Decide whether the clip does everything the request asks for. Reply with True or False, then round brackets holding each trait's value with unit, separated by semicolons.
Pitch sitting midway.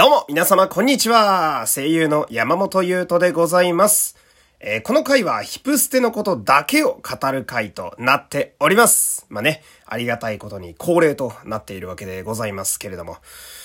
True (170 Hz)